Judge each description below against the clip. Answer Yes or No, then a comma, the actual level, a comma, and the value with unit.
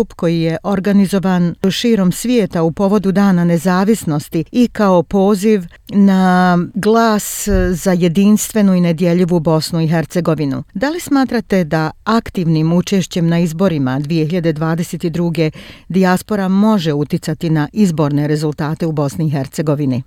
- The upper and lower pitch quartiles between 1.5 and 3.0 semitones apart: No, average, 3.6 semitones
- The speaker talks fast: No, average, 120 wpm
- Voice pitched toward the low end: No, medium, 180 Hz